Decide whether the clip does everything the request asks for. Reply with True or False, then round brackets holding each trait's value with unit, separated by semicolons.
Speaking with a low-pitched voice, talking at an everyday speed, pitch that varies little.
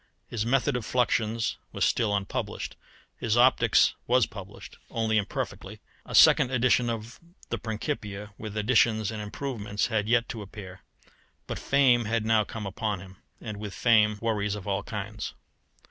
True (110 Hz; 155 wpm; 2.2 semitones)